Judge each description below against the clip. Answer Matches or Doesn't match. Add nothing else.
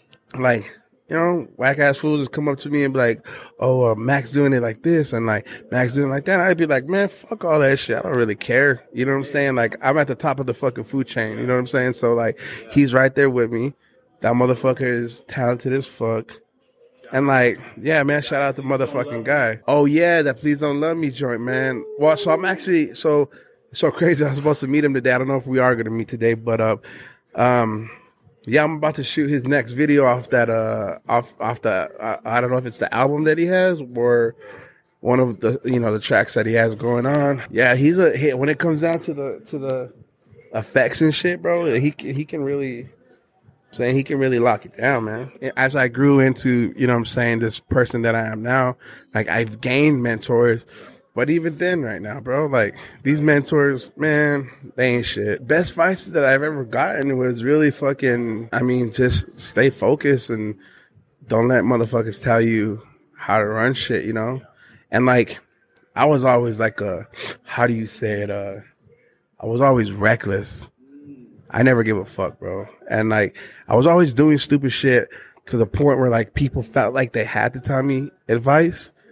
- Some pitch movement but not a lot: Matches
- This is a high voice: Doesn't match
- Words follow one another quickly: Matches